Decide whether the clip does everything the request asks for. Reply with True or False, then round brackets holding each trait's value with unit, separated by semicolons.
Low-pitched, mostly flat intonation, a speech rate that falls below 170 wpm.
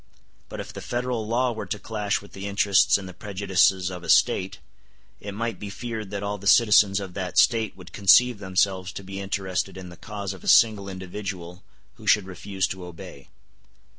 False (100 Hz; 2.0 semitones; 195 wpm)